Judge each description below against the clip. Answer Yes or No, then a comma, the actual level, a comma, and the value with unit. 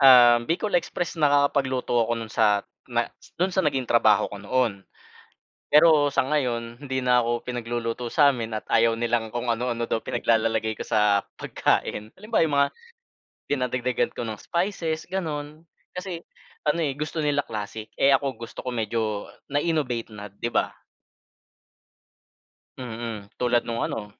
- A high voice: No, low, 125 Hz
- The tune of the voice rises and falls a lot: No, average, 4.3 semitones